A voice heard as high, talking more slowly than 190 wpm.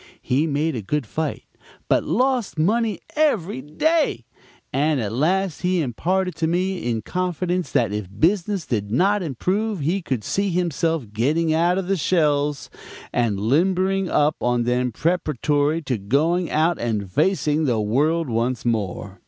No: medium, 155 Hz; average, 150 wpm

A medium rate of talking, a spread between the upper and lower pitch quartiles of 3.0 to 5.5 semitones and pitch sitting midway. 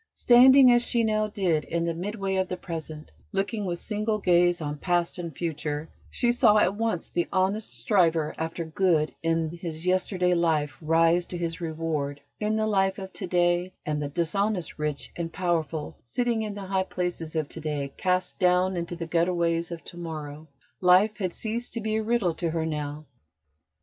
Yes: average, 185 wpm; average, 3.4 semitones; medium, 175 Hz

